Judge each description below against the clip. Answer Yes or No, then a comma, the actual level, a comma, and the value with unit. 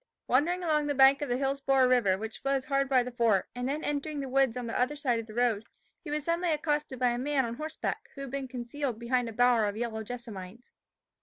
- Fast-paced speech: Yes, fast, 240 wpm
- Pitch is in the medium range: No, very high, 255 Hz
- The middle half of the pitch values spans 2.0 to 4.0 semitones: Yes, average, 3.2 semitones